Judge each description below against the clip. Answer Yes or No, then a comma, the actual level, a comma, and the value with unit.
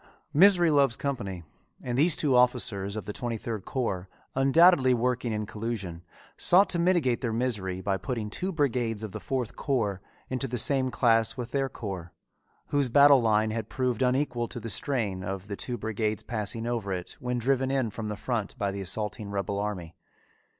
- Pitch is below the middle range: Yes, low, 115 Hz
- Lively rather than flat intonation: No, average, 4.1 semitones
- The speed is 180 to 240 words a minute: Yes, average, 185 wpm